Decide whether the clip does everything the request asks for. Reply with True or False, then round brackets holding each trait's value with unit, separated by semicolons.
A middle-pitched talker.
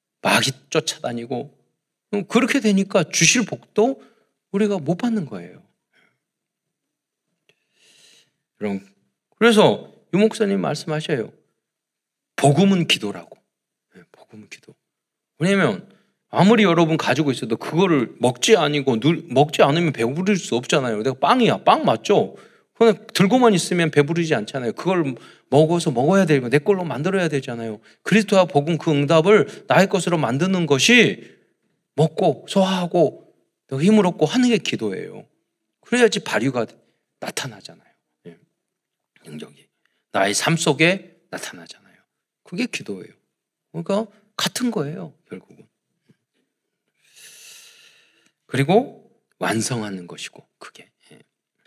True (180 Hz)